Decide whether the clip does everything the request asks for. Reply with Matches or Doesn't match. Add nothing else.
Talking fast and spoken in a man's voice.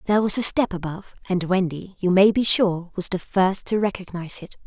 Doesn't match